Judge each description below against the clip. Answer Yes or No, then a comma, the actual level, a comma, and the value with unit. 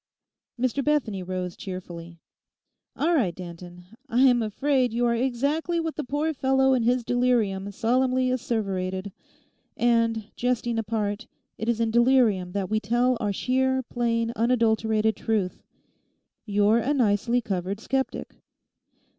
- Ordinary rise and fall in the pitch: Yes, average, 3.9 semitones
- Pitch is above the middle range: Yes, high, 230 Hz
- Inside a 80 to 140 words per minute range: Yes, slow, 135 wpm